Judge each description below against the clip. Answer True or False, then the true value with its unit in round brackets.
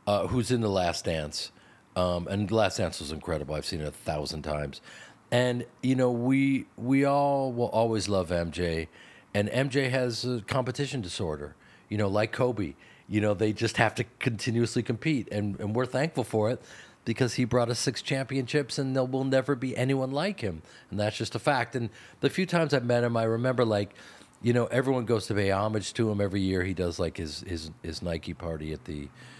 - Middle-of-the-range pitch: False (115 Hz)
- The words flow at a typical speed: False (210 wpm)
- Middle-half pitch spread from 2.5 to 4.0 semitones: False (5.6 semitones)